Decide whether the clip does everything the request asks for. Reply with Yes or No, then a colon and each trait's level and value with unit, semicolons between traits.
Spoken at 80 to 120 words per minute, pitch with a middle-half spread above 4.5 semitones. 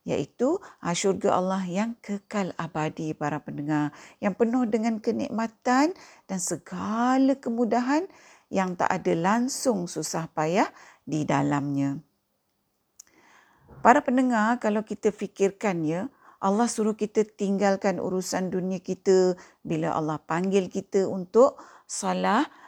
Yes: average, 110 wpm; average, 4.9 semitones